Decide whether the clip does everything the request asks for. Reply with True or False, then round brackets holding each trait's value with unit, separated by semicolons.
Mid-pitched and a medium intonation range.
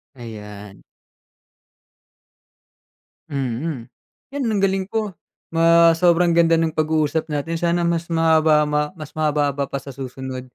True (155 Hz; 3.4 semitones)